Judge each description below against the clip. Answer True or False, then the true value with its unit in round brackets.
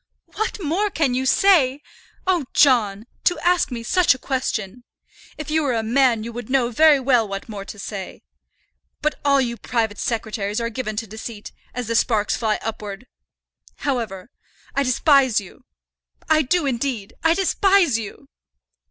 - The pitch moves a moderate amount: True (4.9 semitones)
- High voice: True (245 Hz)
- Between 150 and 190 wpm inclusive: True (160 wpm)